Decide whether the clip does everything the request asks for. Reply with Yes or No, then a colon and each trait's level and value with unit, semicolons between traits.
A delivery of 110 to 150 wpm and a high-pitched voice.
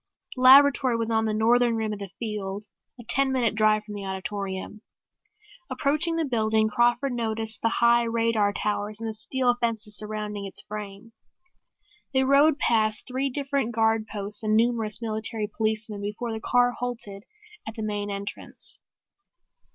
No: average, 160 wpm; high, 220 Hz